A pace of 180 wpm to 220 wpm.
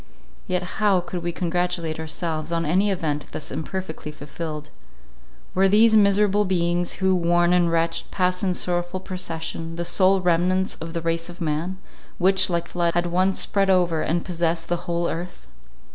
No: average, 170 wpm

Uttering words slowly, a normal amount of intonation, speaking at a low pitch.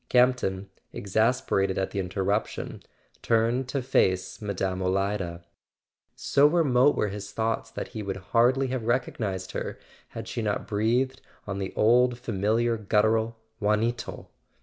Yes: slow, 130 wpm; average, 3.9 semitones; low, 110 Hz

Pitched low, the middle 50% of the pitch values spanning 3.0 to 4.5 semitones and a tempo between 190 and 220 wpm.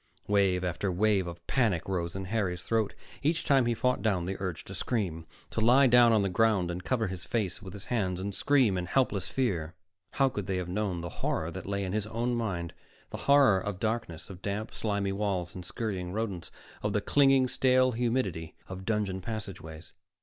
Yes: low, 100 Hz; average, 4.0 semitones; average, 200 wpm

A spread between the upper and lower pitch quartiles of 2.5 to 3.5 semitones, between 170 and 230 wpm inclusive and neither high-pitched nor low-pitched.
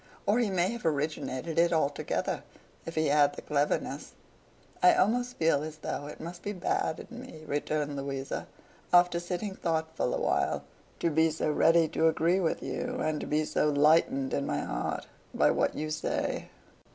Yes: average, 2.9 semitones; average, 175 wpm; medium, 160 Hz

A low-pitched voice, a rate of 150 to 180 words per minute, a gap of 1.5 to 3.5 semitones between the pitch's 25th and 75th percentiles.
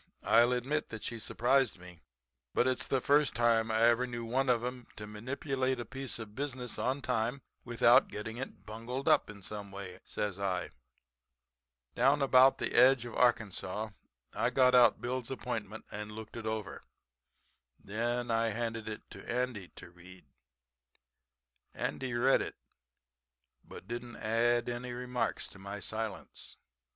Yes: low, 120 Hz; average, 155 wpm; average, 2.8 semitones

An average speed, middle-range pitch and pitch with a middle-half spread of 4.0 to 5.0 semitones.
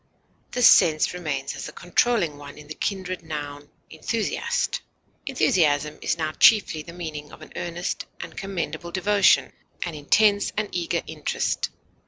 Yes: average, 145 wpm; medium, 170 Hz; average, 4.3 semitones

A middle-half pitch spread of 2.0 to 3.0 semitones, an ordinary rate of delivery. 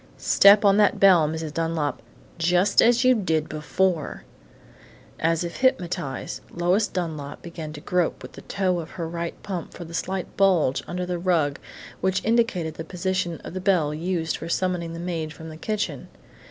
Yes: average, 2.7 semitones; average, 175 wpm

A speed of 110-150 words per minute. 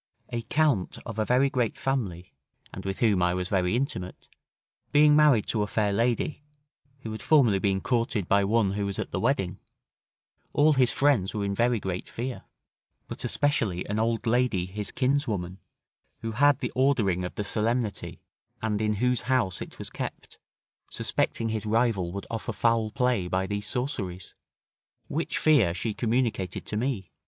No: average, 170 wpm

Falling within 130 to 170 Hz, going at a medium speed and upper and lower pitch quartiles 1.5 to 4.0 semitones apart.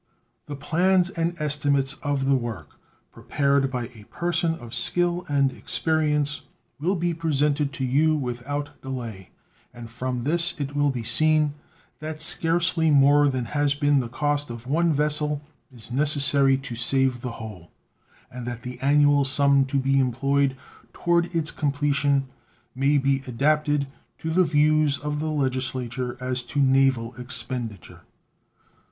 Yes: medium, 140 Hz; average, 145 wpm; average, 2.8 semitones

